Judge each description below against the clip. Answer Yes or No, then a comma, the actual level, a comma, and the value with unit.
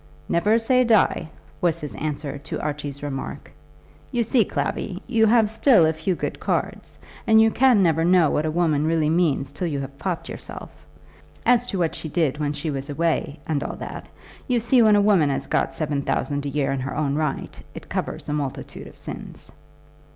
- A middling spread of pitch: No, wide, 6.2 semitones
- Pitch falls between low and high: Yes, medium, 160 Hz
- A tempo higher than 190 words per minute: Yes, average, 200 wpm